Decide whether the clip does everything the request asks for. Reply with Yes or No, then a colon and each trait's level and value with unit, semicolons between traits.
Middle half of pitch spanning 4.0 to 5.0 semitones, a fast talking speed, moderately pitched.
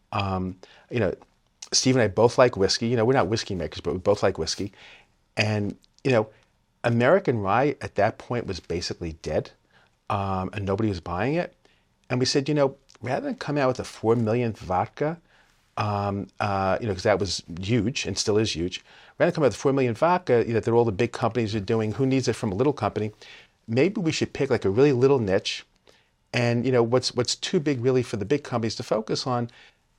No: average, 4.3 semitones; fast, 220 wpm; low, 115 Hz